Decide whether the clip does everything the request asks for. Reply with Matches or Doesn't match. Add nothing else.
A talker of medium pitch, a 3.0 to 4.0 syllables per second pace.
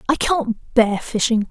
Doesn't match